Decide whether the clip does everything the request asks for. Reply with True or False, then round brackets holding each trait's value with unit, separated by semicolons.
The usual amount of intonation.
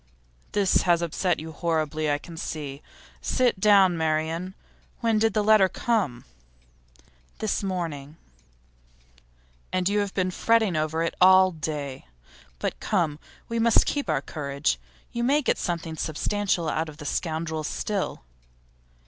True (4.6 semitones)